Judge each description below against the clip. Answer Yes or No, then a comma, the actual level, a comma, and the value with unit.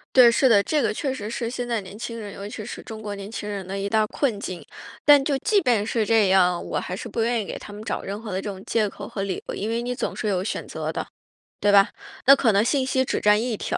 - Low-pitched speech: No, high, 215 Hz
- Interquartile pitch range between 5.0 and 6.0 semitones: No, average, 3.1 semitones